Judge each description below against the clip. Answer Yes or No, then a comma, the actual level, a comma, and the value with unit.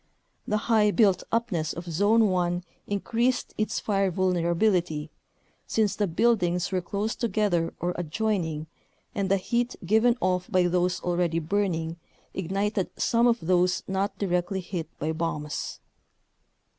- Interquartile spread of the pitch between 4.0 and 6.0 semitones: No, average, 3.5 semitones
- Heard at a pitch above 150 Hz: Yes, medium, 185 Hz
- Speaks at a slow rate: Yes, slow, 130 wpm